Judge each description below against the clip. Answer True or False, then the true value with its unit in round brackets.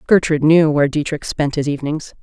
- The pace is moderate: True (190 wpm)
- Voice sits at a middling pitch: True (150 Hz)